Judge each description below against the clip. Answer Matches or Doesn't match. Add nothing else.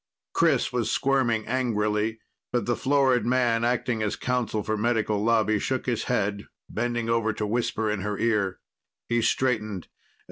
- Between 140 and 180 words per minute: Matches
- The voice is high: Doesn't match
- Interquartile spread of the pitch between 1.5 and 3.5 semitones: Matches